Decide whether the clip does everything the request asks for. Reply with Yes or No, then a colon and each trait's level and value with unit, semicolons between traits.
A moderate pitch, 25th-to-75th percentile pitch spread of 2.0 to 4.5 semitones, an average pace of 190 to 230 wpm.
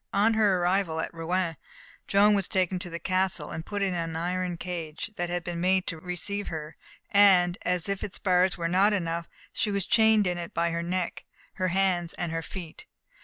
Yes: medium, 180 Hz; narrow, 2.4 semitones; fast, 205 wpm